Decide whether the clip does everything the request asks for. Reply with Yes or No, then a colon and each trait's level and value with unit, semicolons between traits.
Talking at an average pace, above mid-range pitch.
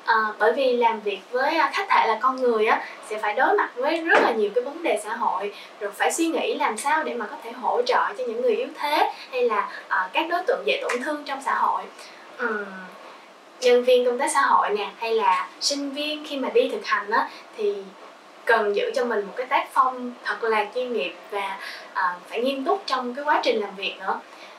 Yes: average, 235 wpm; very high, 300 Hz